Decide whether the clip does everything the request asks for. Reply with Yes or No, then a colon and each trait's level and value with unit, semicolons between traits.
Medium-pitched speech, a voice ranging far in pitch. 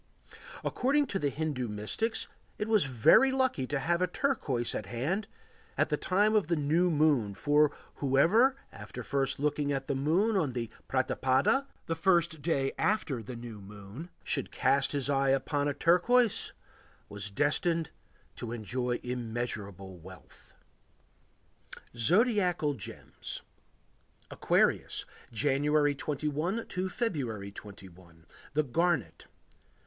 Yes: medium, 145 Hz; wide, 6.5 semitones